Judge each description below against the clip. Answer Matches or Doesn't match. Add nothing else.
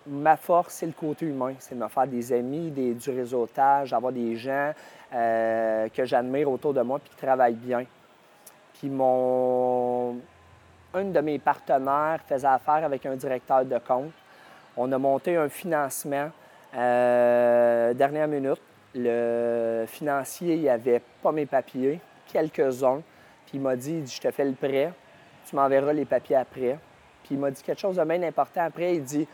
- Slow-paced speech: Doesn't match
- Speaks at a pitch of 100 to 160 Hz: Matches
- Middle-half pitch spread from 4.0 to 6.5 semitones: Doesn't match